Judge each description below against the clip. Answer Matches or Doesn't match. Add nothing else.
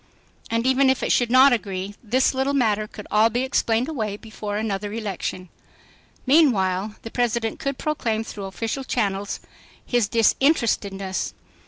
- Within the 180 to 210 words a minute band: Doesn't match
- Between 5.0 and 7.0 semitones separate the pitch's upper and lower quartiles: Doesn't match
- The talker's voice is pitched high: Matches